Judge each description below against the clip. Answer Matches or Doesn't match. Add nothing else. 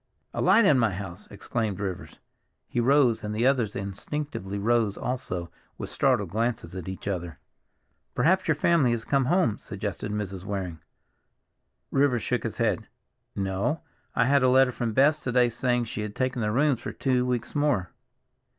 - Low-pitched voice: Matches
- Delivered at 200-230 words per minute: Doesn't match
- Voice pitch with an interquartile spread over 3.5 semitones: Matches